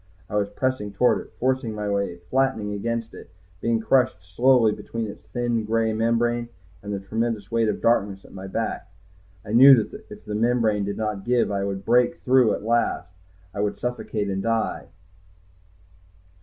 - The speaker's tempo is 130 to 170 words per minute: No, average, 185 wpm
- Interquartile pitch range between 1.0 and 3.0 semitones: Yes, narrow, 2.6 semitones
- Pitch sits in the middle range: No, low, 110 Hz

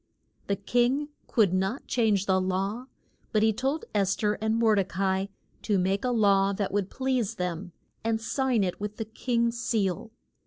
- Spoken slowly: No, average, 185 wpm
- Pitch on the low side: No, high, 210 Hz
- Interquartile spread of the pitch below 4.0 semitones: Yes, average, 3.2 semitones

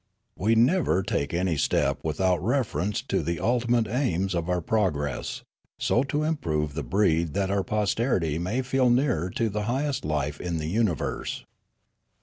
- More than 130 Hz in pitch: No, very low, 95 Hz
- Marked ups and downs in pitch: Yes, wide, 6.6 semitones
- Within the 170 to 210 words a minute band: No, average, 160 wpm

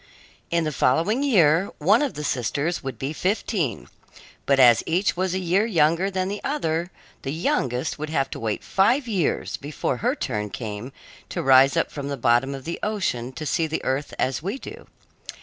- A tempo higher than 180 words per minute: Yes, average, 190 wpm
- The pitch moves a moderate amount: No, wide, 6.0 semitones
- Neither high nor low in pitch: Yes, medium, 160 Hz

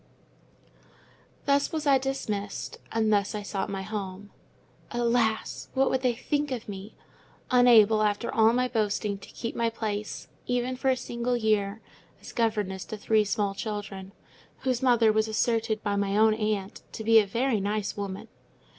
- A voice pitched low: No, high, 220 Hz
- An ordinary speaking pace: Yes, average, 165 wpm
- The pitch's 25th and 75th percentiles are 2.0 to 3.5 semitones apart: Yes, average, 2.8 semitones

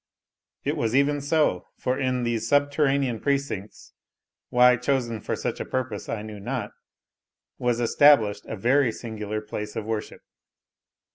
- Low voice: Yes, low, 120 Hz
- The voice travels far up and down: No, average, 4.3 semitones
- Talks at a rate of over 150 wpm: No, average, 140 wpm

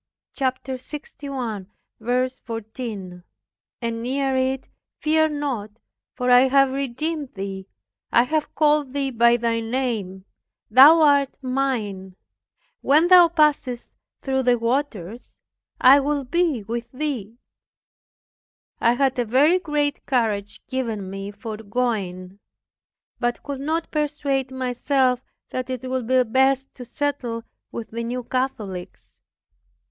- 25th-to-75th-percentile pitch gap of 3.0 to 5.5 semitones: Yes, average, 3.4 semitones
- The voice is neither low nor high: No, very high, 255 Hz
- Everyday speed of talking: No, slow, 120 wpm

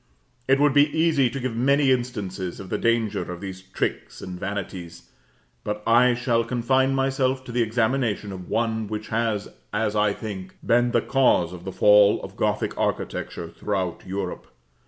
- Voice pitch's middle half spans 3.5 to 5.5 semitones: Yes, average, 4.3 semitones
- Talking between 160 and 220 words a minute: Yes, average, 170 wpm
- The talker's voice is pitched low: Yes, low, 110 Hz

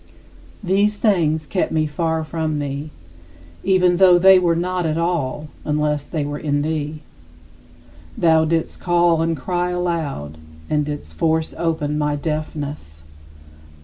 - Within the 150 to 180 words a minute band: No, slow, 135 wpm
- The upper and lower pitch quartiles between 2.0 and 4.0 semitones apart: Yes, average, 2.8 semitones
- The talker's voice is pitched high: No, medium, 160 Hz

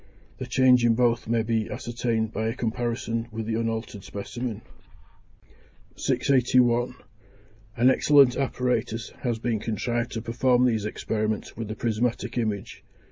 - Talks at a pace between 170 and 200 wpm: No, slow, 135 wpm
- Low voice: Yes, low, 115 Hz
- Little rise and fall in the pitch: Yes, narrow, 1.8 semitones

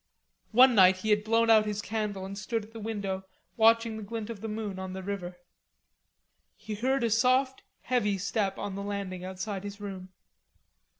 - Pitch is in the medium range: No, high, 210 Hz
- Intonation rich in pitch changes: No, narrow, 2.6 semitones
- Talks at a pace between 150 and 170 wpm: No, average, 185 wpm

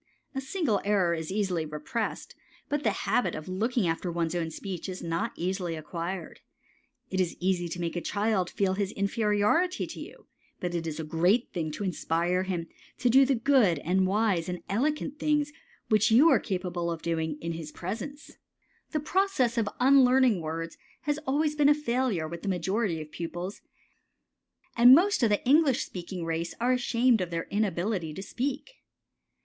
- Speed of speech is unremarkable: Yes, average, 175 wpm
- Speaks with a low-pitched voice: No, high, 195 Hz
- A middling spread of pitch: No, wide, 6.6 semitones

